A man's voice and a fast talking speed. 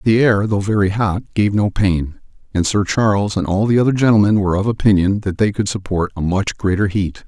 Yes: male; fast, 225 wpm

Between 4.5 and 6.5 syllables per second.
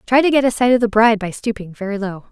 No: 6.9 syllables/s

